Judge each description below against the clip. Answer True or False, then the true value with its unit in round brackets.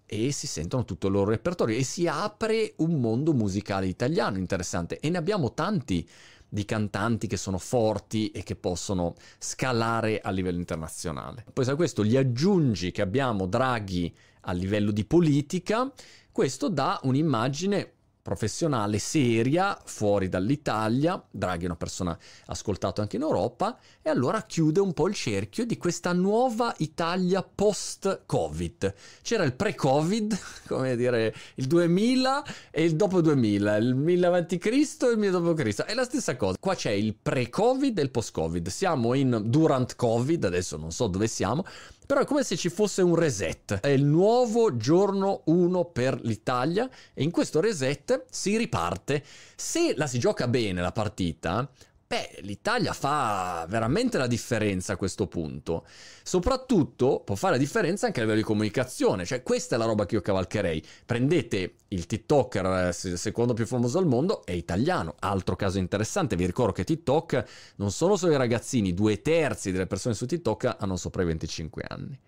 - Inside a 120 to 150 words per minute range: False (165 wpm)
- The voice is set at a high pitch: False (125 Hz)